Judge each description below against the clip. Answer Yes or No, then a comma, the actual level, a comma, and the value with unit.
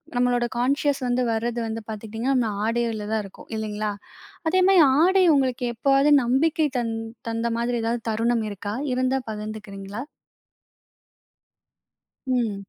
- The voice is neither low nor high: No, high, 235 Hz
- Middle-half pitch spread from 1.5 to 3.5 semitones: Yes, average, 3.0 semitones